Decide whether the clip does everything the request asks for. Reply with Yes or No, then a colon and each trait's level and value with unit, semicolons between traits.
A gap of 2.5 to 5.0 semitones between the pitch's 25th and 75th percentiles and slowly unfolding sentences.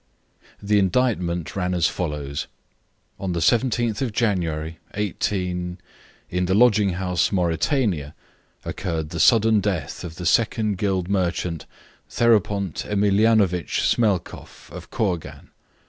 Yes: average, 3.4 semitones; slow, 115 wpm